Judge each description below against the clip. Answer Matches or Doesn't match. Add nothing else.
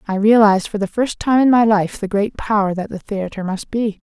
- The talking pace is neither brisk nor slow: Doesn't match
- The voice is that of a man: Doesn't match